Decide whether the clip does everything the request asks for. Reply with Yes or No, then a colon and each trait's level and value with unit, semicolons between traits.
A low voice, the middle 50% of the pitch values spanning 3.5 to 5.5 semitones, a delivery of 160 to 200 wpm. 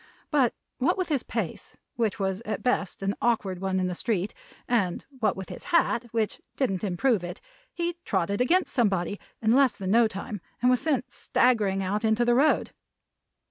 No: high, 220 Hz; average, 4.6 semitones; average, 180 wpm